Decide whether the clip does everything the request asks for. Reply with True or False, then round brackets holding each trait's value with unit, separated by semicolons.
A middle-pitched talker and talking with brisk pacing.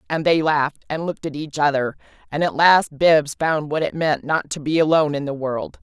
True (150 Hz; 235 wpm)